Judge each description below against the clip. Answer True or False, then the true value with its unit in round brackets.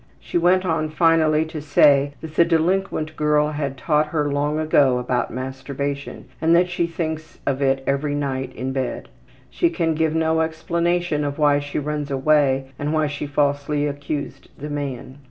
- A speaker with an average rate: True (170 wpm)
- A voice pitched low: False (150 Hz)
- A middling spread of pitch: False (2.2 semitones)